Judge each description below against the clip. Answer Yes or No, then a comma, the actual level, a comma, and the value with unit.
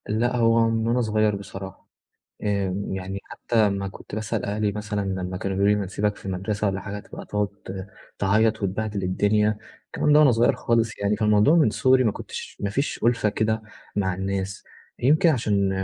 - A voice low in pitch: Yes, low, 105 Hz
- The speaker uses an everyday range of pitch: No, narrow, 2.2 semitones